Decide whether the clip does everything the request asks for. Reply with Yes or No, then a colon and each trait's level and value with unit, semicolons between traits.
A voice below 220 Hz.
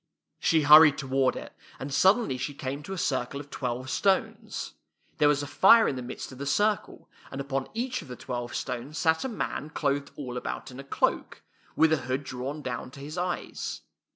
Yes: medium, 140 Hz